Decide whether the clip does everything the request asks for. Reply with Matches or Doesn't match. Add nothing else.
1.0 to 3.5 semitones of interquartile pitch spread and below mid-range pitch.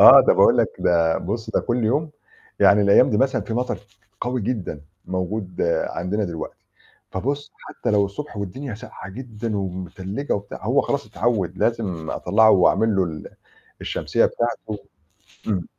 Doesn't match